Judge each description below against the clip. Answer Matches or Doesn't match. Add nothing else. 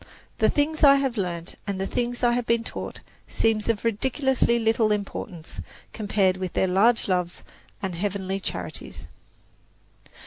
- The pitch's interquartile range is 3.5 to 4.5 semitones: Matches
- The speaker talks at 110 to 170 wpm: Matches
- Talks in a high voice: Matches